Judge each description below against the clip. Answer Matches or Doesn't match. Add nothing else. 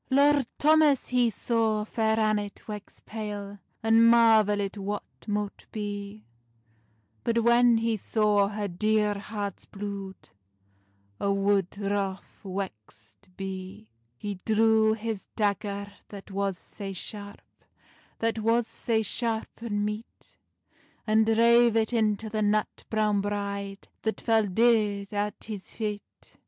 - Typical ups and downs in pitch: Doesn't match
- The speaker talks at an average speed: Doesn't match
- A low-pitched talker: Doesn't match